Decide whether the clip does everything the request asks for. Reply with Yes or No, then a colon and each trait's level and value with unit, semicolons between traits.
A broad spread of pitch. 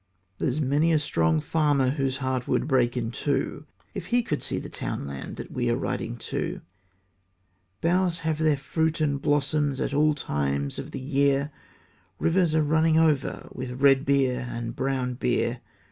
No: average, 3.4 semitones